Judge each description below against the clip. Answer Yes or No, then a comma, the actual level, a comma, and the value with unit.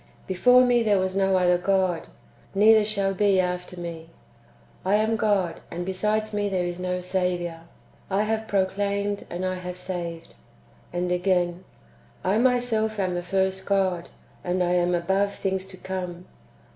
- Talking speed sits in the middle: Yes, average, 165 wpm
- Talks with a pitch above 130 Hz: Yes, high, 190 Hz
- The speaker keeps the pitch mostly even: Yes, narrow, 2.2 semitones